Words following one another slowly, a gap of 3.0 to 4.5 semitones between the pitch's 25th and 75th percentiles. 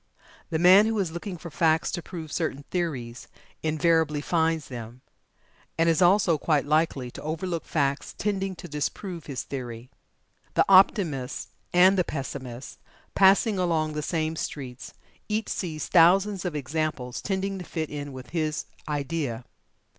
No: average, 145 wpm; average, 3.9 semitones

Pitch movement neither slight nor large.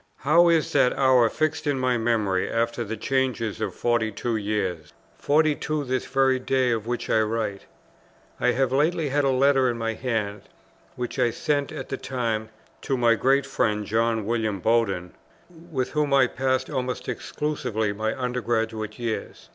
Yes: average, 3.3 semitones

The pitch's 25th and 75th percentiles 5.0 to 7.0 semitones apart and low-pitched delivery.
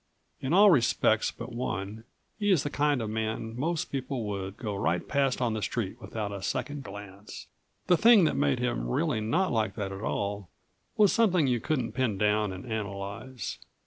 Yes: wide, 5.5 semitones; low, 115 Hz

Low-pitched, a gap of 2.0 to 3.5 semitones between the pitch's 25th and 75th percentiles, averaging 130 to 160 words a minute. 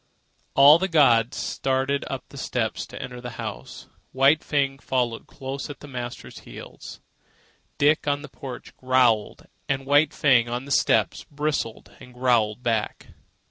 Yes: low, 130 Hz; average, 2.7 semitones; average, 150 wpm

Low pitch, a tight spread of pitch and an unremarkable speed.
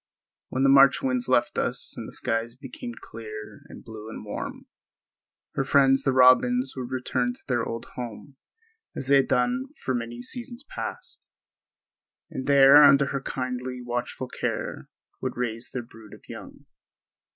Yes: low, 125 Hz; narrow, 2.3 semitones; average, 160 wpm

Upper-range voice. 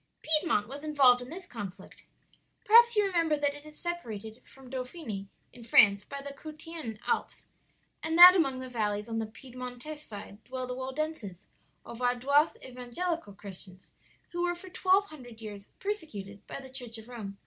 Yes: very high, 255 Hz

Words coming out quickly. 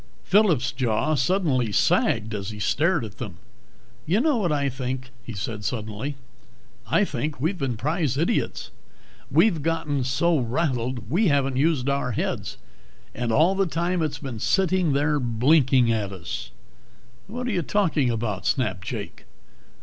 No: average, 150 wpm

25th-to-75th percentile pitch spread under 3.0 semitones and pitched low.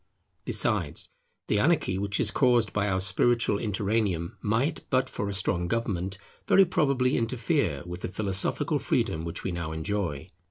No: average, 4.6 semitones; low, 100 Hz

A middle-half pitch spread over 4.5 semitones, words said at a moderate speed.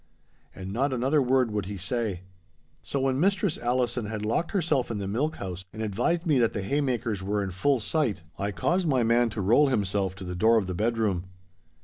No: average, 5.0 semitones; fast, 210 wpm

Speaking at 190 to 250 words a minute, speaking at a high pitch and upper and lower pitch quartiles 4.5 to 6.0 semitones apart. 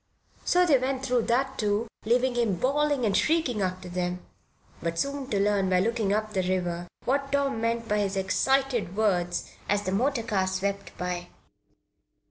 No: average, 170 wpm; high, 215 Hz; wide, 5.6 semitones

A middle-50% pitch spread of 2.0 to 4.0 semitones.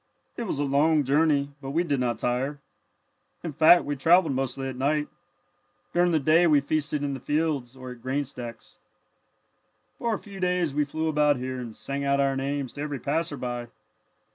Yes: average, 2.9 semitones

